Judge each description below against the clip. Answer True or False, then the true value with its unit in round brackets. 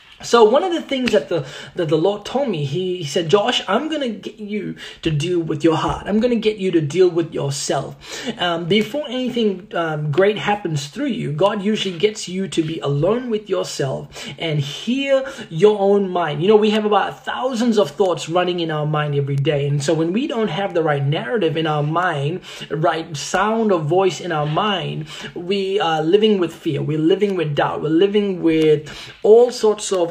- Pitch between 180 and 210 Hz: True (185 Hz)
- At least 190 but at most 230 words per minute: True (205 wpm)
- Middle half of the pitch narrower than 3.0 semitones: False (4.6 semitones)